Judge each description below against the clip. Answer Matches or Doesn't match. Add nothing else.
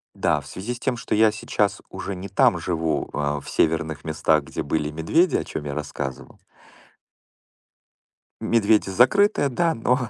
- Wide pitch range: Matches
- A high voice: Doesn't match